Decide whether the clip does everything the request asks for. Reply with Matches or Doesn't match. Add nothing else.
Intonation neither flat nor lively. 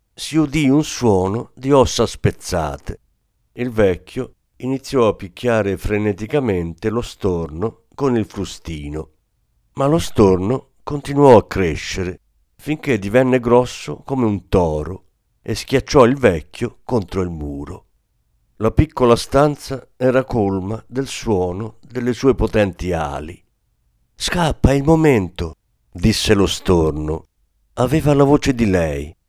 Doesn't match